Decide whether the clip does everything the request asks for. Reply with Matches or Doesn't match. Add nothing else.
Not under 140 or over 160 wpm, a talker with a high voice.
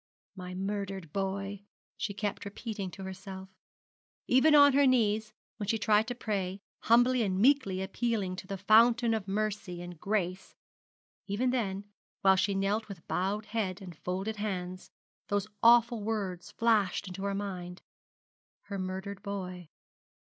Matches